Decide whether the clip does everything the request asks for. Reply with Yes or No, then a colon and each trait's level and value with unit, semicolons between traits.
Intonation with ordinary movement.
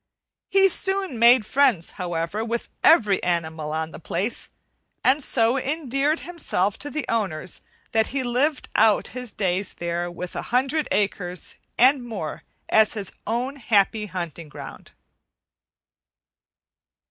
No: wide, 6.8 semitones